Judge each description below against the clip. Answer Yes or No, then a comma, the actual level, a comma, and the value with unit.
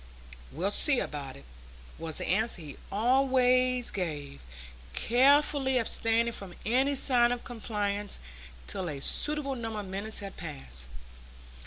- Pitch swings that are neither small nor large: No, wide, 6.0 semitones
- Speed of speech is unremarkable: No, slow, 130 wpm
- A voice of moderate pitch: No, high, 225 Hz